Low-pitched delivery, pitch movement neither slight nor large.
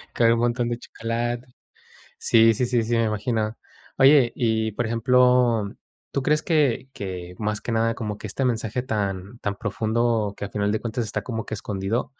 No: low, 115 Hz; narrow, 2.2 semitones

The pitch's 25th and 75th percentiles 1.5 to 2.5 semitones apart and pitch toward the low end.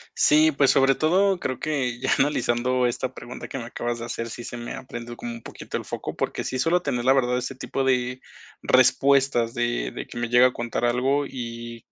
Yes: narrow, 2.2 semitones; low, 125 Hz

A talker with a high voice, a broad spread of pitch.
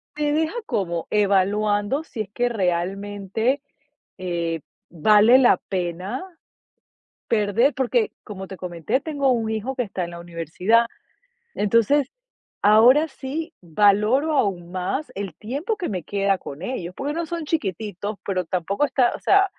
Yes: high, 210 Hz; wide, 6.2 semitones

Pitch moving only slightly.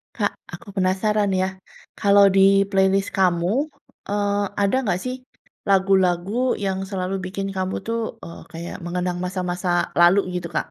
Yes: narrow, 1.8 semitones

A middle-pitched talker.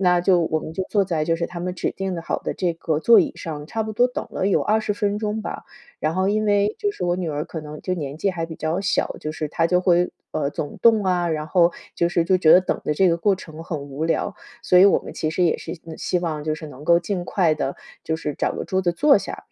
Yes: medium, 175 Hz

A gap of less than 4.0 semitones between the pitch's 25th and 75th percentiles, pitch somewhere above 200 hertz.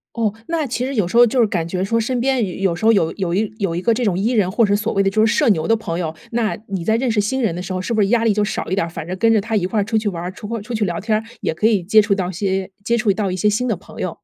Yes: average, 3.5 semitones; high, 210 Hz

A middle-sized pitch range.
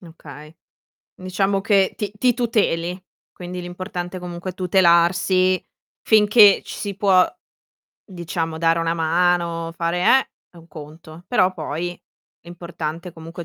No: narrow, 2.0 semitones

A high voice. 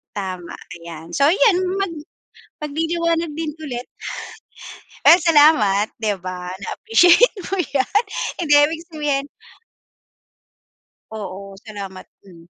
Yes: very high, 285 Hz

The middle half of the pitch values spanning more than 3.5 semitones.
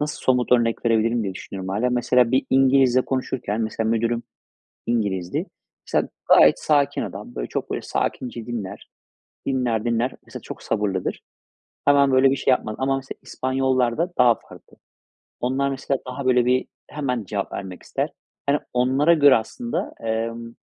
No: average, 2.8 semitones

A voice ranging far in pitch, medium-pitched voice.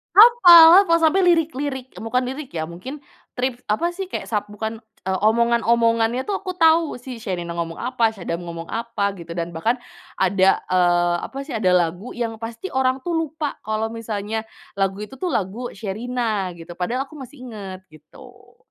No: wide, 5.8 semitones; high, 230 Hz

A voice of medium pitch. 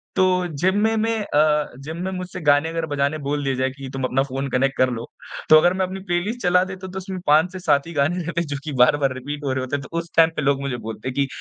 Yes: medium, 150 Hz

